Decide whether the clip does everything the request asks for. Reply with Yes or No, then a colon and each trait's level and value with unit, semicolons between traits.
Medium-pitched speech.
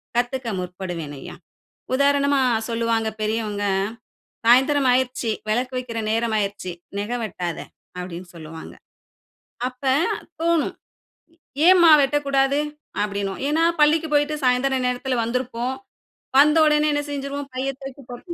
No: very high, 250 Hz